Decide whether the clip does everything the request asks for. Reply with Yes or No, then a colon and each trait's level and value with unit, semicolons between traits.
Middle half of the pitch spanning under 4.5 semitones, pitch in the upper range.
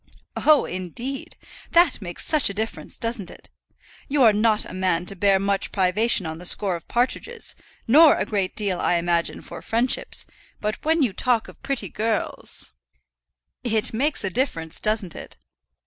No: average, 5.3 semitones; high, 215 Hz